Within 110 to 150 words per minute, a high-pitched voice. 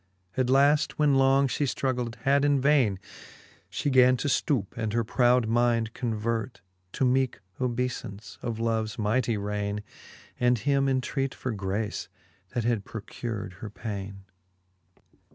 No: slow, 135 wpm; low, 120 Hz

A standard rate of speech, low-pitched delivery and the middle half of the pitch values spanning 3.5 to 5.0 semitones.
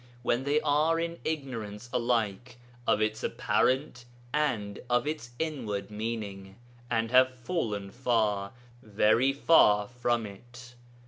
No: slow, 125 wpm; low, 120 Hz; average, 3.9 semitones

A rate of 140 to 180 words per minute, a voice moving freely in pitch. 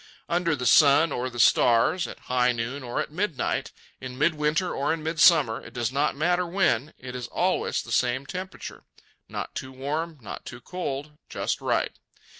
No: average, 170 wpm; average, 4.8 semitones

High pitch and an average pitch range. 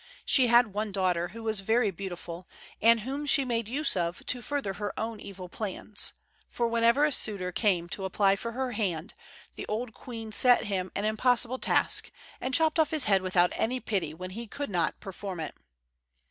Yes: high, 215 Hz; average, 4.4 semitones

